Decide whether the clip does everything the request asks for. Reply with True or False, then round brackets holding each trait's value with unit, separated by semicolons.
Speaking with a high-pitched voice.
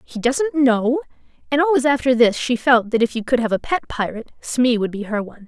True (250 Hz)